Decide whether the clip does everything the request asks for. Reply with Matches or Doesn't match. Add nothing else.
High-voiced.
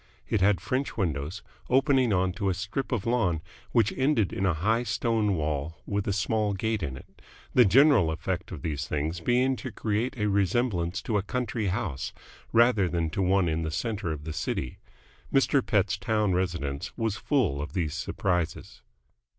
Doesn't match